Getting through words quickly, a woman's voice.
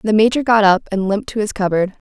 Yes: fast, 255 wpm; female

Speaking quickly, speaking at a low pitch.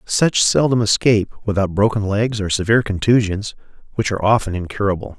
No: average, 150 wpm; low, 105 Hz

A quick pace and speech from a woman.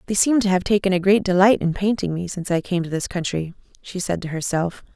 Yes: fast, 255 wpm; female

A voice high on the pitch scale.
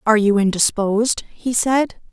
Yes: high, 220 Hz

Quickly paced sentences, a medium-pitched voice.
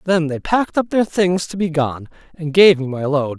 Yes: fast, 250 wpm; medium, 165 Hz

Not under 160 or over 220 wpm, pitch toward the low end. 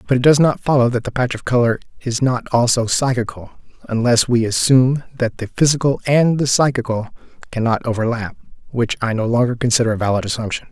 Yes: average, 185 wpm; low, 120 Hz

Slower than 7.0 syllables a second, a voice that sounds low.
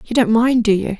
No: 5.6 syllables/s; high, 220 Hz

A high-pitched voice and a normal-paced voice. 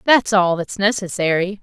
Yes: high, 195 Hz; average, 145 wpm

